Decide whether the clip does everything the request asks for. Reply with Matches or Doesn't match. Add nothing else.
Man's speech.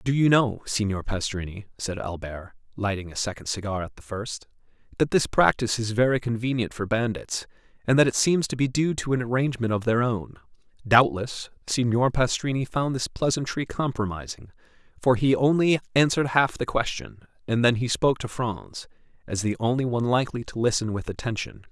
Matches